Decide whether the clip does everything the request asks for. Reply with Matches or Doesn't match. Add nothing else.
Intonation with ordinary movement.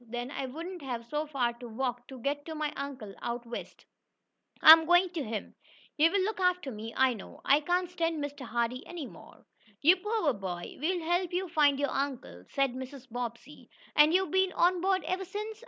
Doesn't match